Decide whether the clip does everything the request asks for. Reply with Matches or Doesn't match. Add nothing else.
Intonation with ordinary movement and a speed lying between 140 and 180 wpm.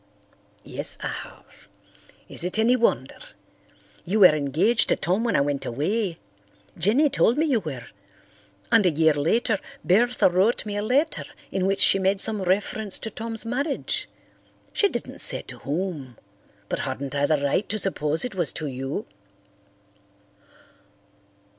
Doesn't match